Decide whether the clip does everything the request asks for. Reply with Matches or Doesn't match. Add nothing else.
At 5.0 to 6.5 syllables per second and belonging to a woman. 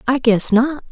Doesn't match